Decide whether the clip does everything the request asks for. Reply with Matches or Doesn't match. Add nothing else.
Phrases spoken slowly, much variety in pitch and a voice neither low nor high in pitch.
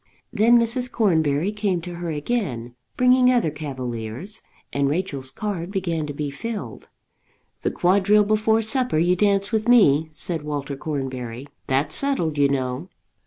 Doesn't match